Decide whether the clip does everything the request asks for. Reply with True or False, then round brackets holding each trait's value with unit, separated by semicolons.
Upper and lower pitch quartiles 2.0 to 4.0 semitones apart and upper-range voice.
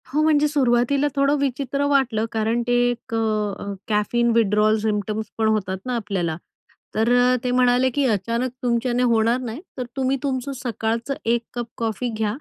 True (2.8 semitones; 235 Hz)